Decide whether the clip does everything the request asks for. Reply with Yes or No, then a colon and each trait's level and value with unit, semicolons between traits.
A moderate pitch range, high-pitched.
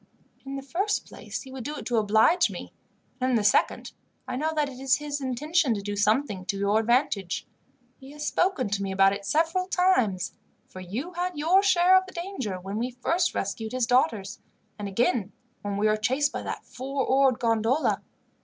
No: wide, 6.4 semitones; very high, 255 Hz